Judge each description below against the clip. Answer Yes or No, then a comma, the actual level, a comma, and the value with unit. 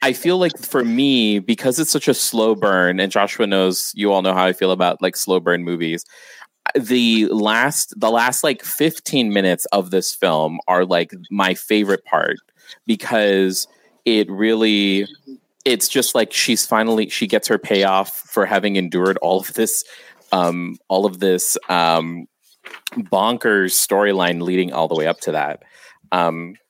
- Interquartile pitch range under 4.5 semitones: Yes, average, 3.3 semitones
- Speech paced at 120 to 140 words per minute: No, average, 165 wpm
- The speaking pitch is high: No, very low, 95 Hz